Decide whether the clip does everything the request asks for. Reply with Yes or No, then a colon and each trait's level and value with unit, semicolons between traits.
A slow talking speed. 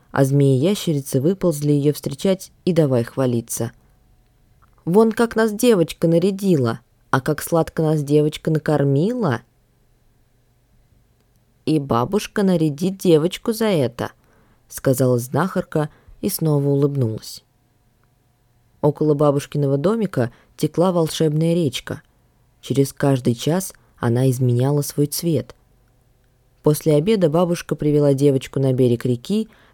Yes: slow, 105 wpm